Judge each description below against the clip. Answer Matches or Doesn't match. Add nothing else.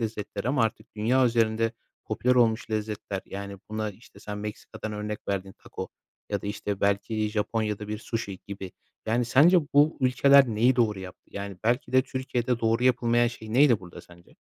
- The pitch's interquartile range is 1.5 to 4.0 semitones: Matches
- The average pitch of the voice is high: Doesn't match